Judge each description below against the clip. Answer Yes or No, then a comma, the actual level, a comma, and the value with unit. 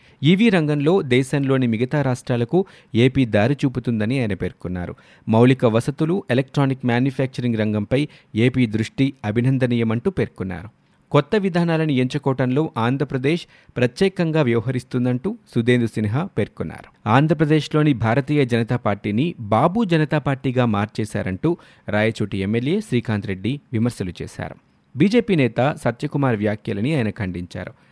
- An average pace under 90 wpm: No, average, 105 wpm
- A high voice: No, low, 130 Hz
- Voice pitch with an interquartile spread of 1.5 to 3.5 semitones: No, average, 4.8 semitones